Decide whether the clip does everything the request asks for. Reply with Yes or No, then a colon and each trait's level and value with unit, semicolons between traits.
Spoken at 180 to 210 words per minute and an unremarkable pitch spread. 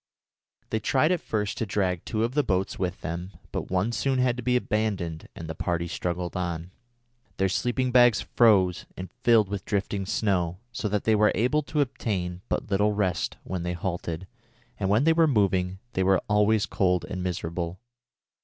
Yes: average, 185 wpm; average, 3.8 semitones